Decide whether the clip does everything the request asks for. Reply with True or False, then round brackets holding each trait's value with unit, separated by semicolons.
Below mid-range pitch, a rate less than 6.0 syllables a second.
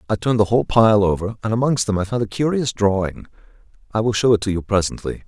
False (105 Hz; 6.6 syllables/s)